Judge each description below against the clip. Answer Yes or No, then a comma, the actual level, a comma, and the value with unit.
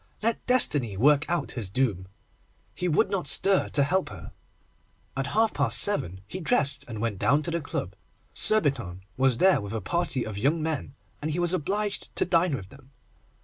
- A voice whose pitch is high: No, medium, 140 Hz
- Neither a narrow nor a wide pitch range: No, wide, 7.3 semitones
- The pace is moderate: Yes, average, 190 wpm